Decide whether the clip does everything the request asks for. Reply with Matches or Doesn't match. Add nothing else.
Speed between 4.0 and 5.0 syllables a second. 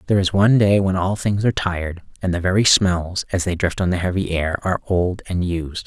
Doesn't match